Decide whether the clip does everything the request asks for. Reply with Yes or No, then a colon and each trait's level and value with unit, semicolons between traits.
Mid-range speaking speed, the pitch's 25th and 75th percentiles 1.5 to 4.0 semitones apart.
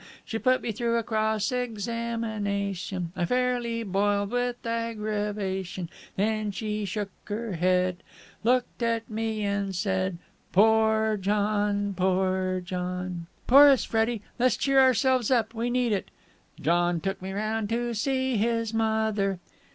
No: slow, 130 wpm; average, 3.1 semitones